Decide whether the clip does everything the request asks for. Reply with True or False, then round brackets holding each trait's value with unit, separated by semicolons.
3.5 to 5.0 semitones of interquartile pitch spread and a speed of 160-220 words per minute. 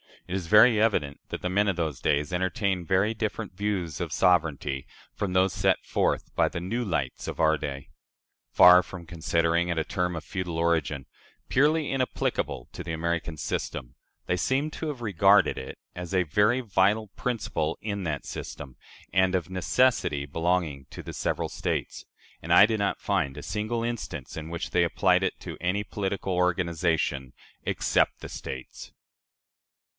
True (4.1 semitones; 170 wpm)